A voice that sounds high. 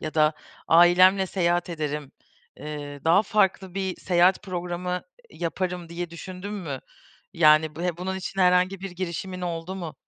No: medium, 175 Hz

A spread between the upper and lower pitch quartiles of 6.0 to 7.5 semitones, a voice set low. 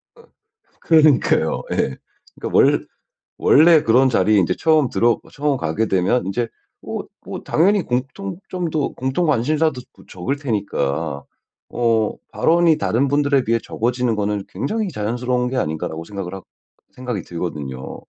Yes: wide, 6.8 semitones; low, 125 Hz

